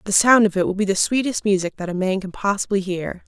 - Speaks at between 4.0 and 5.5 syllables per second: No, 6.2 syllables/s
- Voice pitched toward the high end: Yes, high, 195 Hz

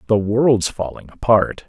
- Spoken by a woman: No, male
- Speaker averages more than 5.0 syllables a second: No, 4.1 syllables/s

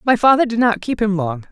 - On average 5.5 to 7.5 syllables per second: Yes, 5.8 syllables/s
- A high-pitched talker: Yes, high, 245 Hz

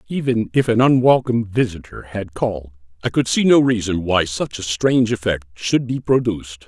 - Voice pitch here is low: Yes, low, 110 Hz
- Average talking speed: Yes, average, 180 wpm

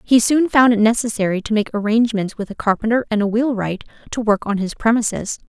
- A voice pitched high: Yes, high, 220 Hz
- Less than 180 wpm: No, average, 195 wpm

